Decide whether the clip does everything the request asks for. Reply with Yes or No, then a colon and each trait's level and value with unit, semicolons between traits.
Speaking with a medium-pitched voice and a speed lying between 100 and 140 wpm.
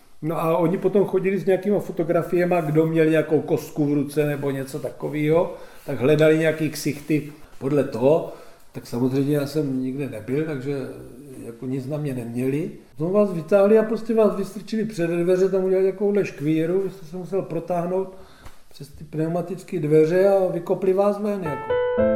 No: medium, 165 Hz; fast, 170 wpm